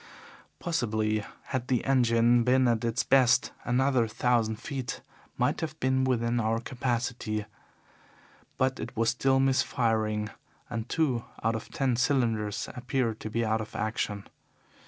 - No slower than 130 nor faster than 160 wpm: Yes, average, 140 wpm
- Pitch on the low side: Yes, low, 120 Hz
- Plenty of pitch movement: No, average, 2.7 semitones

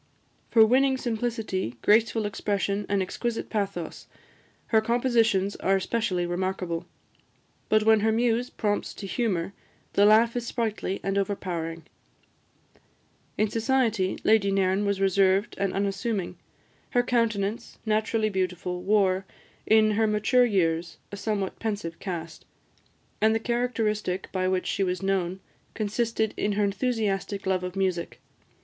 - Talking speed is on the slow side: Yes, slow, 130 wpm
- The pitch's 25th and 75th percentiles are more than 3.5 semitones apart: No, average, 2.9 semitones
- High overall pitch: Yes, high, 205 Hz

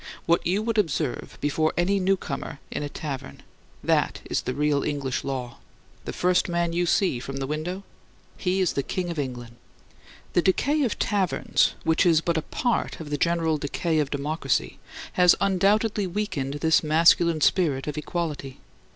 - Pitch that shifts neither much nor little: Yes, average, 4.0 semitones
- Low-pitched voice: No, medium, 165 Hz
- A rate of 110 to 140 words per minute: No, average, 170 wpm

